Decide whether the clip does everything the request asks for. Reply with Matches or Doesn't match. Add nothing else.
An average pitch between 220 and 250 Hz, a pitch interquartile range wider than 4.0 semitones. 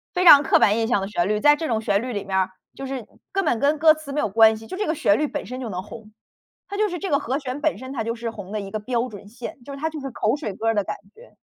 Matches